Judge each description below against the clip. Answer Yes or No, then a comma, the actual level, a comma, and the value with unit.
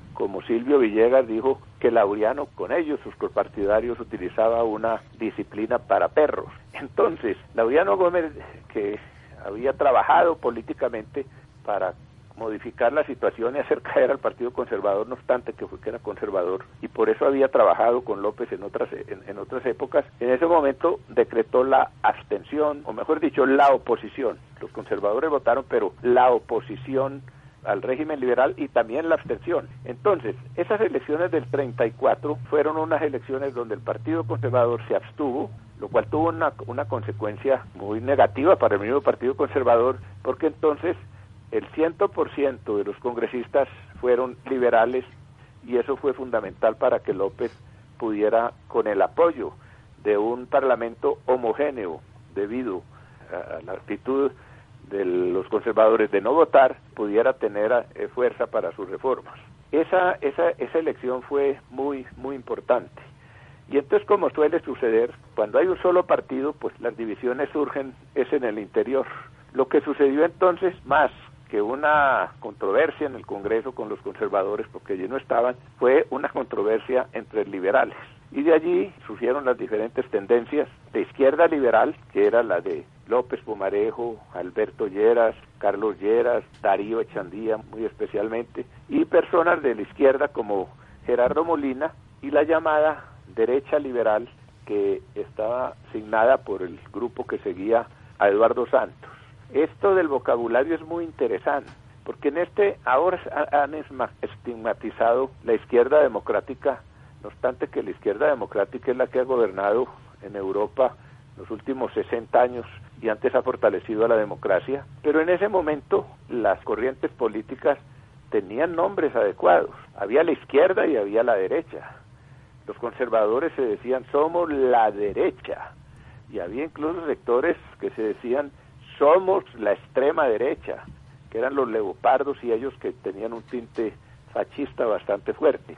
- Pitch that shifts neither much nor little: No, wide, 8.8 semitones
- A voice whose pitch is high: No, medium, 140 Hz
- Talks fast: No, average, 145 wpm